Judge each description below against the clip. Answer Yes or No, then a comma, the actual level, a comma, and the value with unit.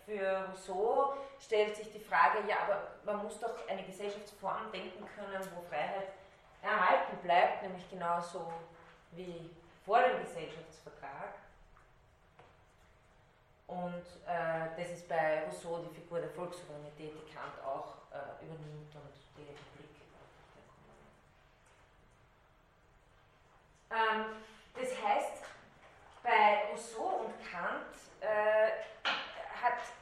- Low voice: No, medium, 180 Hz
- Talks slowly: Yes, slow, 105 wpm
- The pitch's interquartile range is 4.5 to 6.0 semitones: Yes, average, 5.0 semitones